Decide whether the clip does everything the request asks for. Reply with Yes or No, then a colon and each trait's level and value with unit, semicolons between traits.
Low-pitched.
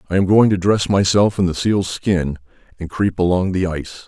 Yes: very low, 95 Hz